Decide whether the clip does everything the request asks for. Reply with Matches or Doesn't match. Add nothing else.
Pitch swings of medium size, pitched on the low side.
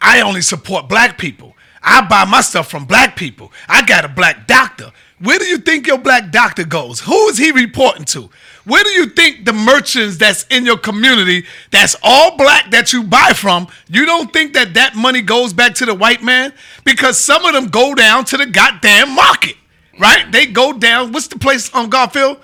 Doesn't match